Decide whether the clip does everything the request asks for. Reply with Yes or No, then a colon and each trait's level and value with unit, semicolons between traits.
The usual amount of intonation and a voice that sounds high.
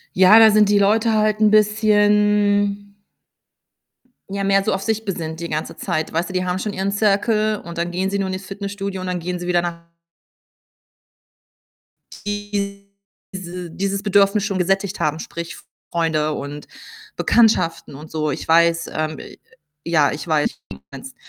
Yes: average, 3.5 semitones; high, 195 Hz